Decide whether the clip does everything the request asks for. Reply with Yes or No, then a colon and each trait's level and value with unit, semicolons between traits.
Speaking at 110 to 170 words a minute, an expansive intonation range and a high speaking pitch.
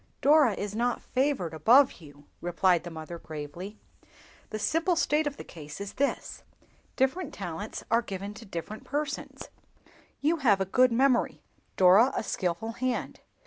Yes: average, 145 wpm; wide, 7.3 semitones; high, 215 Hz